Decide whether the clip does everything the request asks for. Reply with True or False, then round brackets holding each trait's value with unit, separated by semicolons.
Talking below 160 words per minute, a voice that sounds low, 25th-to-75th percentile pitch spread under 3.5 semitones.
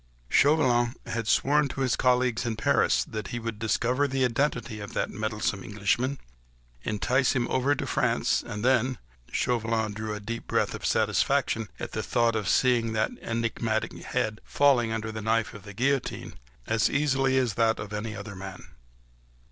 False (170 wpm; 115 Hz; 2.9 semitones)